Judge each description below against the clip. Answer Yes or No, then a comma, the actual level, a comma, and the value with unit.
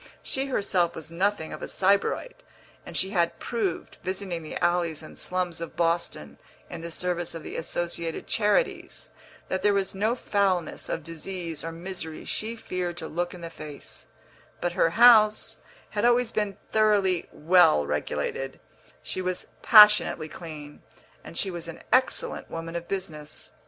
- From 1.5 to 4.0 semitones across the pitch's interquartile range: Yes, average, 3.6 semitones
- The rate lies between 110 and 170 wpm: Yes, average, 155 wpm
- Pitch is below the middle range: No, medium, 180 Hz